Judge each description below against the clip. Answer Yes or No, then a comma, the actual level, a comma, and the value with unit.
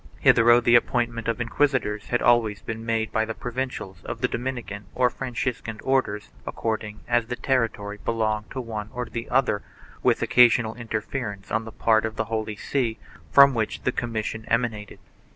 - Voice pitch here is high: No, low, 115 Hz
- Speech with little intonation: Yes, narrow, 2.0 semitones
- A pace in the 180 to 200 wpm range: No, average, 170 wpm